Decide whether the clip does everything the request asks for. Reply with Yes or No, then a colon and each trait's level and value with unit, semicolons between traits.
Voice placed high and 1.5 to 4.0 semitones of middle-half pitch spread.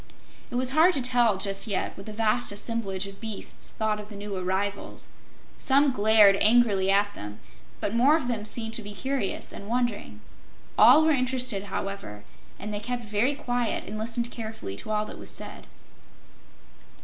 Yes: high, 215 Hz; average, 3.4 semitones